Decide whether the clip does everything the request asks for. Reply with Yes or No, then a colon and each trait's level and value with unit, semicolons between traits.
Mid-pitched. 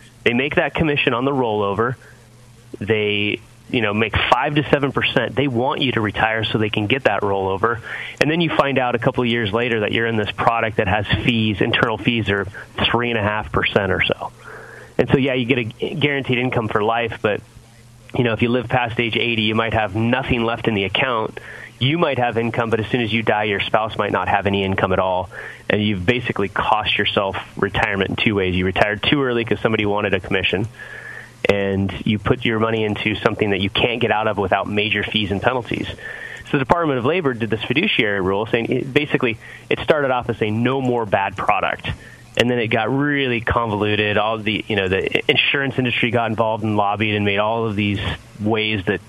No: low, 115 Hz